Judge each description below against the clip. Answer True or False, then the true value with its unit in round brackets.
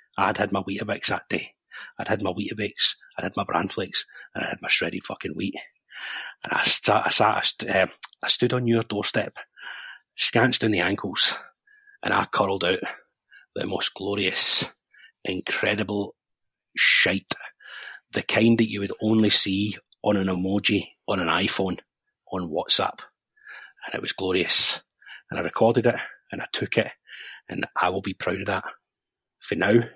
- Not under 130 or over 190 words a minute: True (170 wpm)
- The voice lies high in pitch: False (105 Hz)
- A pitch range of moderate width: True (3.7 semitones)